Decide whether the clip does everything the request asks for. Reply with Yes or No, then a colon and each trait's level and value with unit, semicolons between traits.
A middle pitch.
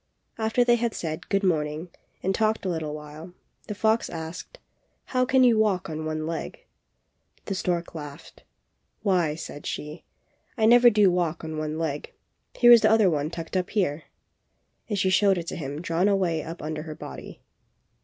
Yes: medium, 175 Hz